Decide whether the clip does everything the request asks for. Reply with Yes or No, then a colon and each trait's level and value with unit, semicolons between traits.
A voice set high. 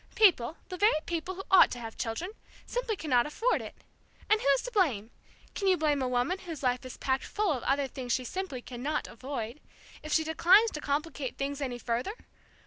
Yes: very high, 290 Hz